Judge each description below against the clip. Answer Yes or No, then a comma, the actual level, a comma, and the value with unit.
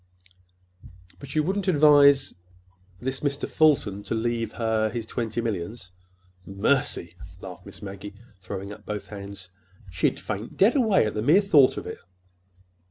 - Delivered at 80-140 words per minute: Yes, slow, 135 wpm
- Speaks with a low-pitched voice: Yes, low, 115 Hz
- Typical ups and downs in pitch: No, wide, 5.9 semitones